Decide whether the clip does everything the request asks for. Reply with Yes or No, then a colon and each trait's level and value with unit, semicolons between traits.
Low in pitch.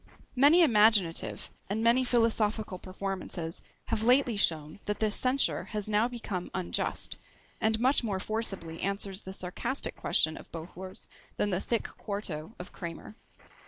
No: high, 210 Hz